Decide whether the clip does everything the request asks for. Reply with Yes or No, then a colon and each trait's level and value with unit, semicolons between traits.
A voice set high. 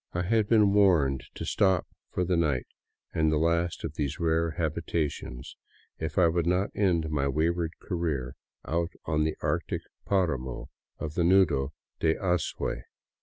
No: very low, 80 Hz